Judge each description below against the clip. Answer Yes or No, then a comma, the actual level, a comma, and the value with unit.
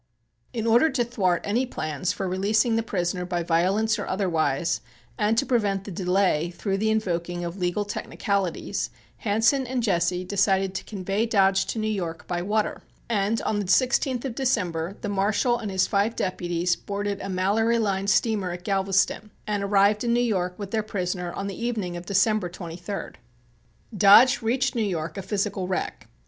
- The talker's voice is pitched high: Yes, high, 200 Hz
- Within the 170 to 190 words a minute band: Yes, average, 175 wpm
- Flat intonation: No, average, 3.3 semitones